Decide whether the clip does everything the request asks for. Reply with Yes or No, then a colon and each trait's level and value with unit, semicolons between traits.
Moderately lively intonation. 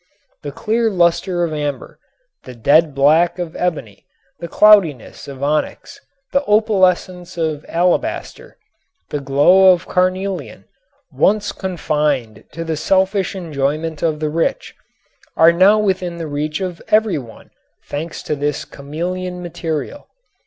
Yes: average, 3.9 semitones